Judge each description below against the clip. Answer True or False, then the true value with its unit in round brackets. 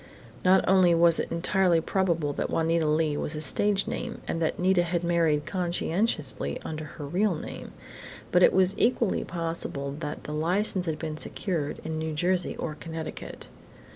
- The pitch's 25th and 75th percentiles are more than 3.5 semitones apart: False (2.8 semitones)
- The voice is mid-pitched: True (165 Hz)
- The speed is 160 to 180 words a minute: True (170 wpm)